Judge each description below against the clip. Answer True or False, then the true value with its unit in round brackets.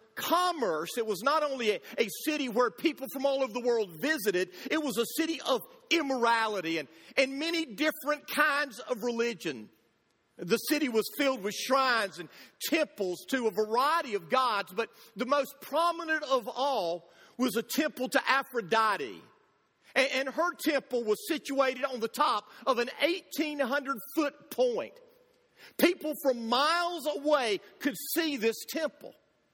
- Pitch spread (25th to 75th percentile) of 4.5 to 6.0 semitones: True (4.9 semitones)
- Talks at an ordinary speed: True (150 wpm)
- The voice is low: False (270 Hz)